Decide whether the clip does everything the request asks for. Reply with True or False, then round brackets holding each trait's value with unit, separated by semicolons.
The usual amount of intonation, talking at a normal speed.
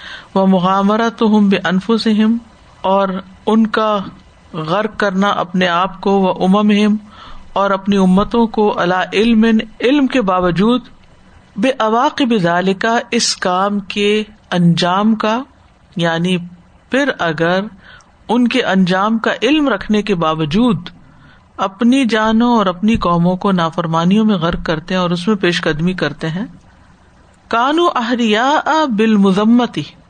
True (3.6 semitones; 135 wpm)